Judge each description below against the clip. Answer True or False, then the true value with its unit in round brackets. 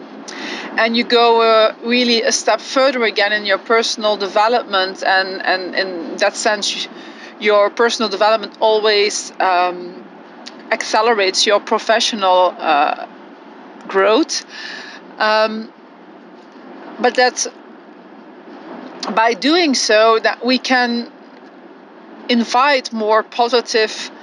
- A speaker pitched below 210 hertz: False (235 Hz)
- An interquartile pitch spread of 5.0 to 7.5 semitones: True (5.6 semitones)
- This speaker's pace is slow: True (100 wpm)